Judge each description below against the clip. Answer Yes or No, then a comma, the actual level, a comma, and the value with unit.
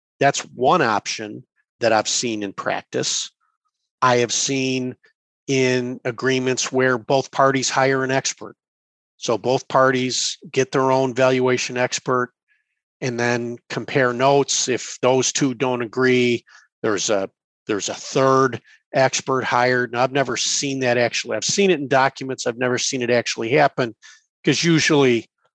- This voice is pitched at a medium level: No, low, 130 Hz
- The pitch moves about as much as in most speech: No, narrow, 1.6 semitones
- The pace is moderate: Yes, average, 145 wpm